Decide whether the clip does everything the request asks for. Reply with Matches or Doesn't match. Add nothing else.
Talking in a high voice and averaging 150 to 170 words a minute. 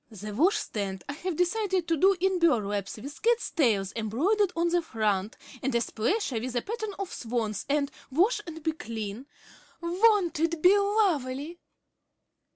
Matches